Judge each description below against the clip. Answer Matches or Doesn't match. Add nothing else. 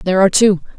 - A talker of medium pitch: Doesn't match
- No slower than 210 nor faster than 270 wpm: Matches